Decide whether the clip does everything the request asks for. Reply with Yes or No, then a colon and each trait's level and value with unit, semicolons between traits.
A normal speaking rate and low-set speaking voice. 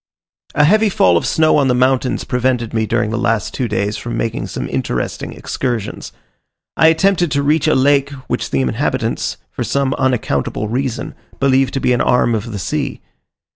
Yes: average, 180 wpm; low, 125 Hz